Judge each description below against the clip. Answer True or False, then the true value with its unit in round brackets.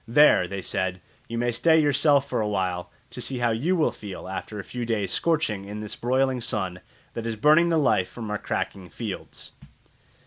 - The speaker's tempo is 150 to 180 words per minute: False (200 wpm)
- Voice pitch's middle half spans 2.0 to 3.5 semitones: False (5.5 semitones)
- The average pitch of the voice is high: False (115 Hz)